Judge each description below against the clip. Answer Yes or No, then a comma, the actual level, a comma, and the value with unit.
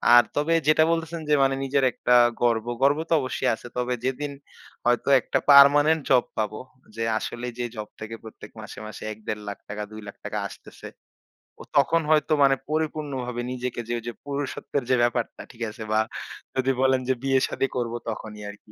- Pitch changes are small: No, average, 3.8 semitones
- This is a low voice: Yes, low, 125 Hz